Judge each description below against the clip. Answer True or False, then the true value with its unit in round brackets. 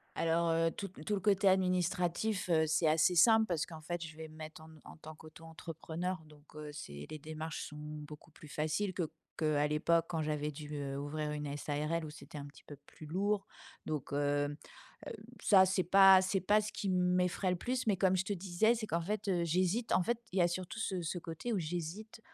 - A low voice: False (170 Hz)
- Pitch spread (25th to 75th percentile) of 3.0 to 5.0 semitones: True (3.5 semitones)